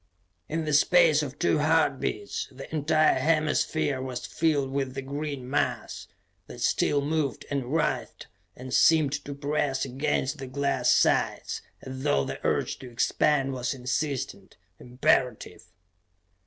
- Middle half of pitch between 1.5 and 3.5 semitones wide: Yes, average, 2.7 semitones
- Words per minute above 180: No, average, 140 wpm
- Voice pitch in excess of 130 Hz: Yes, medium, 140 Hz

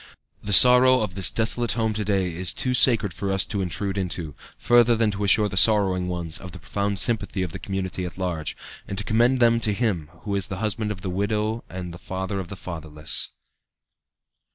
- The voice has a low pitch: Yes, low, 100 Hz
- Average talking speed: No, fast, 210 wpm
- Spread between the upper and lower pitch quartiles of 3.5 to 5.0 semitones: No, average, 3.0 semitones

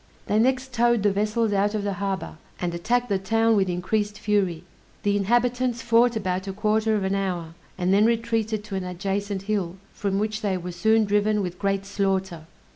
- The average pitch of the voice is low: No, high, 205 Hz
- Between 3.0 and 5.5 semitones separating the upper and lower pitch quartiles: No, narrow, 2.4 semitones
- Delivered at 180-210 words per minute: Yes, average, 195 wpm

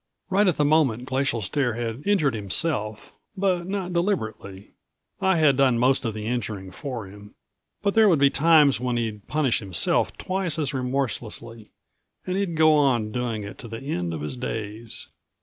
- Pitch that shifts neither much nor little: No, wide, 6.3 semitones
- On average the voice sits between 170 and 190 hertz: No, low, 125 Hz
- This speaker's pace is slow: No, average, 175 wpm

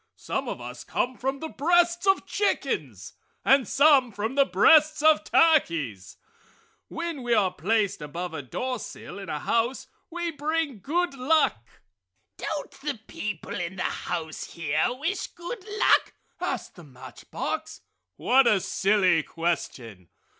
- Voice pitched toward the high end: Yes, high, 245 Hz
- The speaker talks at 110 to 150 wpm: Yes, average, 140 wpm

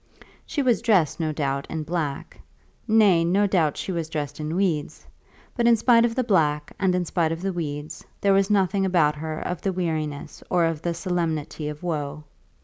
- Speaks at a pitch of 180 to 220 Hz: No, medium, 170 Hz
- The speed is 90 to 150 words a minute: No, average, 195 wpm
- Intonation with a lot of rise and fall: No, average, 4.1 semitones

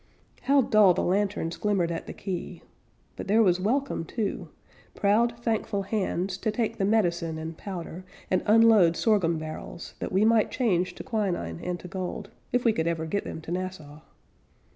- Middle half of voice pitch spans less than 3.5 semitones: No, average, 4.1 semitones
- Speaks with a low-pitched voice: No, high, 190 Hz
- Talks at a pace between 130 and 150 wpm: No, average, 175 wpm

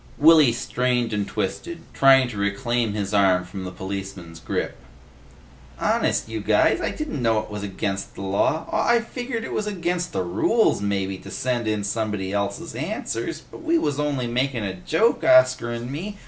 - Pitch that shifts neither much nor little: No, wide, 6.6 semitones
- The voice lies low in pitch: Yes, low, 115 Hz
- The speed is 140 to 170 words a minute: No, average, 180 wpm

